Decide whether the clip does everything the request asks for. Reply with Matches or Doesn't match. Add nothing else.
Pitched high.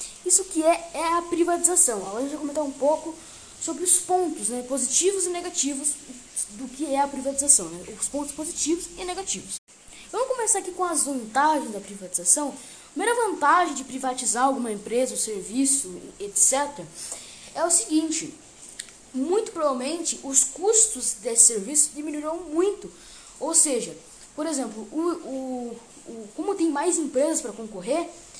Matches